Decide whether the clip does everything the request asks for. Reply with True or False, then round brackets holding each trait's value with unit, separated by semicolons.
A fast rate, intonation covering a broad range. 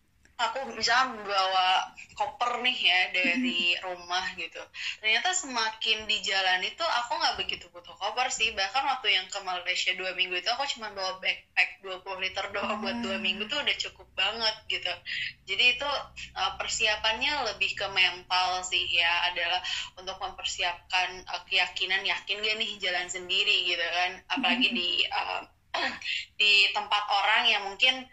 False (150 wpm; 3.4 semitones)